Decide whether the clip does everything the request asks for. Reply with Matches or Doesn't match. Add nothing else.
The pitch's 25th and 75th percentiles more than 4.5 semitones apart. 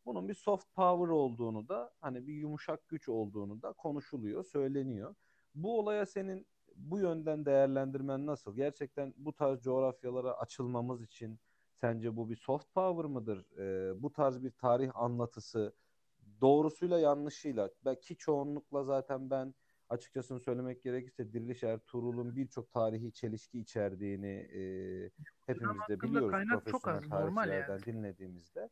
Doesn't match